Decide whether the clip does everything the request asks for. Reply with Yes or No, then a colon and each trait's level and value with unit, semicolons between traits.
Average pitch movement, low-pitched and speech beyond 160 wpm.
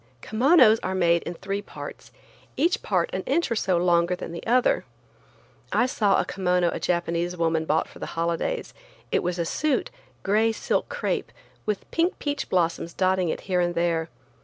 No: average, 4.5 semitones; medium, 180 Hz; average, 180 wpm